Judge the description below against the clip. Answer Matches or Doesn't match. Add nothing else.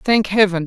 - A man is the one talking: Doesn't match